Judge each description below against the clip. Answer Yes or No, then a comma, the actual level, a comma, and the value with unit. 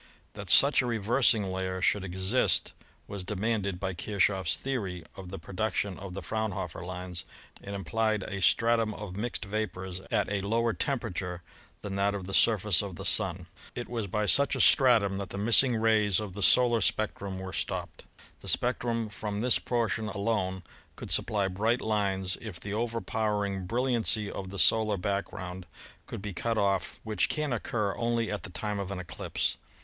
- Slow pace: No, average, 180 wpm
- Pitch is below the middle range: Yes, low, 100 Hz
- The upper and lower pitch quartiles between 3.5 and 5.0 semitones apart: No, average, 3.0 semitones